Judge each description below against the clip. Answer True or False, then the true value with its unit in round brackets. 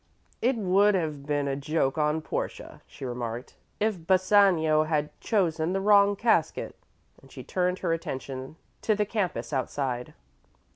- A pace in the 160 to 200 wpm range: False (145 wpm)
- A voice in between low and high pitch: True (160 Hz)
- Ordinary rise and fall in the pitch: False (5.7 semitones)